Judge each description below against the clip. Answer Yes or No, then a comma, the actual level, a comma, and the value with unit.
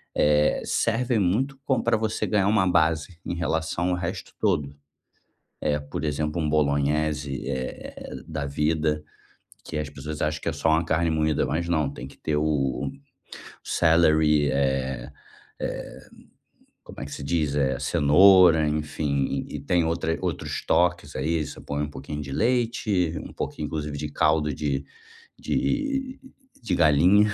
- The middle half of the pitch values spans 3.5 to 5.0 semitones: No, average, 3.1 semitones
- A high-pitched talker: No, very low, 75 Hz